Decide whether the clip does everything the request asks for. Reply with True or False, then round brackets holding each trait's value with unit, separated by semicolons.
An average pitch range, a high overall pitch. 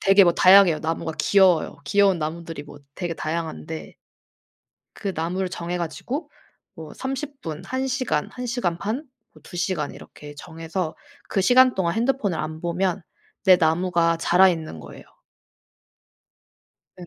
False (3.6 semitones; 175 Hz)